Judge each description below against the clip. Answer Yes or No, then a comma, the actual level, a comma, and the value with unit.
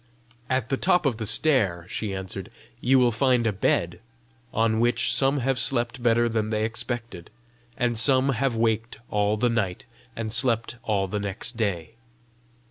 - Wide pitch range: No, average, 2.8 semitones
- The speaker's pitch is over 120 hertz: No, low, 115 Hz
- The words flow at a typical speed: Yes, average, 165 wpm